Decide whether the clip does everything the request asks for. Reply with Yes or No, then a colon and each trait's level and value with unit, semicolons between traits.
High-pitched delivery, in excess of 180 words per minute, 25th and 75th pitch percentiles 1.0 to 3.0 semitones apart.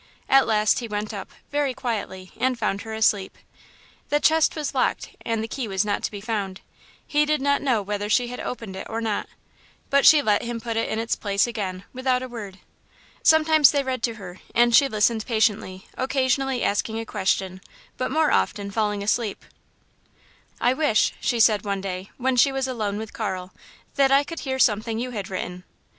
No: high, 225 Hz; average, 195 wpm; average, 4.2 semitones